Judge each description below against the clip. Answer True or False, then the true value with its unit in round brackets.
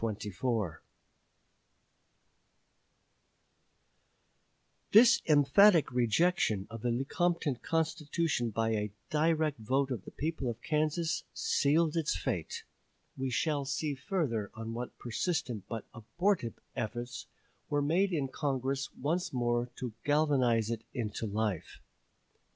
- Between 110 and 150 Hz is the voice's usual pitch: True (135 Hz)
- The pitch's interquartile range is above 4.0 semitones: True (5.3 semitones)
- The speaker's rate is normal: False (105 wpm)